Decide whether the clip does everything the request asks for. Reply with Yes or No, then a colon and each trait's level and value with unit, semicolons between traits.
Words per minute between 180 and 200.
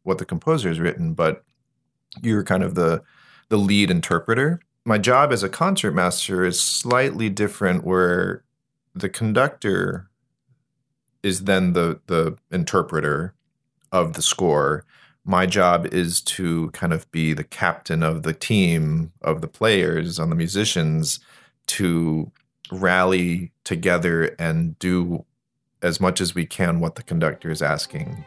No: average, 140 wpm